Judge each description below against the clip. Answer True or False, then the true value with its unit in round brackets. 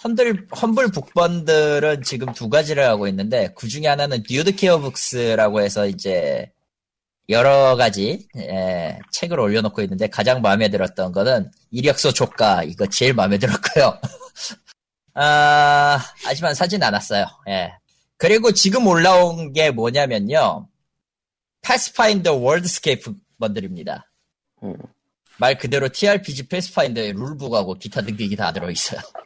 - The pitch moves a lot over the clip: True (7.5 semitones)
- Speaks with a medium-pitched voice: True (145 Hz)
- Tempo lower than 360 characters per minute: True (300 characters per minute)